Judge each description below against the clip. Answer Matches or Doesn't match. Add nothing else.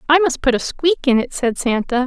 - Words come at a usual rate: Doesn't match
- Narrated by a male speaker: Doesn't match